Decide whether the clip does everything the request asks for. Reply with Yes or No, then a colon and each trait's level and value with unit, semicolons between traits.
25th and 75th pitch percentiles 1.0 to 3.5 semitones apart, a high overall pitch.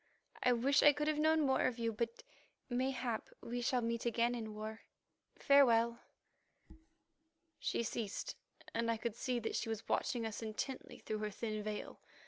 Yes: narrow, 2.4 semitones; high, 235 Hz